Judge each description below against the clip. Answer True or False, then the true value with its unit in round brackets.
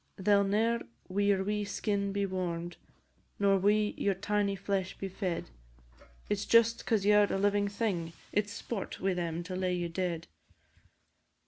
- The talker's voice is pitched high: True (200 Hz)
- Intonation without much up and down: True (2.0 semitones)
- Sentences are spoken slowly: False (170 wpm)